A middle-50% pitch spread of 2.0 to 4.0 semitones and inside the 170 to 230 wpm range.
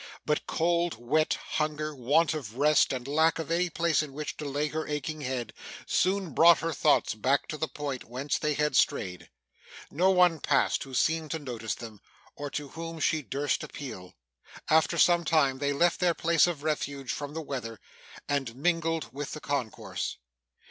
Yes: average, 3.0 semitones; average, 180 wpm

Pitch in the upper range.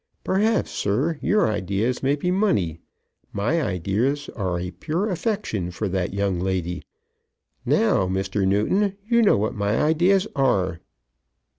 No: low, 105 Hz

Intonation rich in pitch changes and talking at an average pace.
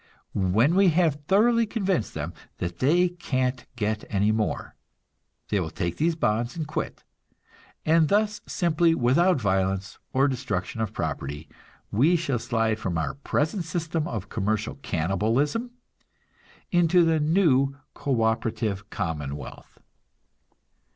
No: wide, 8.2 semitones; slow, 125 wpm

